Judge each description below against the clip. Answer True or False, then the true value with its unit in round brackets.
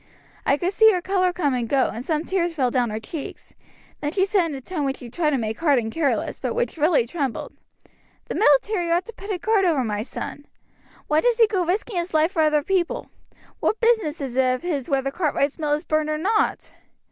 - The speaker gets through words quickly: True (230 wpm)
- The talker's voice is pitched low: False (315 Hz)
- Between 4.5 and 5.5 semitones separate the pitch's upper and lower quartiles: True (5.2 semitones)